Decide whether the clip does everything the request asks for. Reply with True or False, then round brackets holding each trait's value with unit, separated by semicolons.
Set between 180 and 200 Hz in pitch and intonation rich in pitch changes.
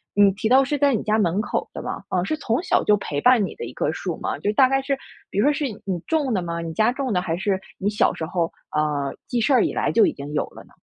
False (210 Hz; 7.0 semitones)